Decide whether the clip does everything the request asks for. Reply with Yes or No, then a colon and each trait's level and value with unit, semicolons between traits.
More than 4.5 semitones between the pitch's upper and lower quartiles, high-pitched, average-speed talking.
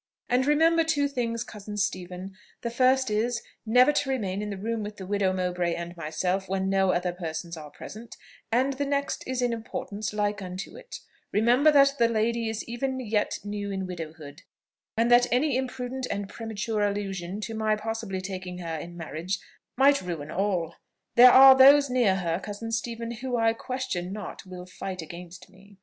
Yes: average, 5.0 semitones; high, 210 Hz; average, 180 wpm